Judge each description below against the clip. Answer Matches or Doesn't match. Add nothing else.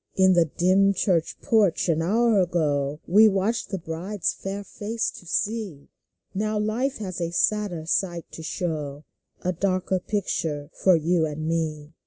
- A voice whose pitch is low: Doesn't match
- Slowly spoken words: Doesn't match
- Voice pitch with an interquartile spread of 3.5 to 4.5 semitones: Matches